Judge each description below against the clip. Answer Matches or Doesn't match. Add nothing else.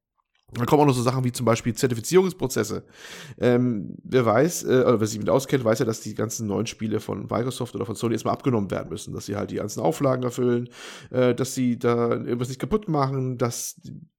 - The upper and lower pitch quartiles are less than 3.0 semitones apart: Matches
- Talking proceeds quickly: Matches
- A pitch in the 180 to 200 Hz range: Doesn't match